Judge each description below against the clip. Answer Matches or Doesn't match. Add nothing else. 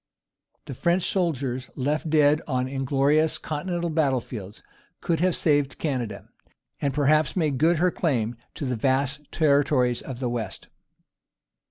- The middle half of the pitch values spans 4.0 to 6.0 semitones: Doesn't match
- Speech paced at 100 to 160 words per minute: Matches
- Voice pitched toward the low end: Doesn't match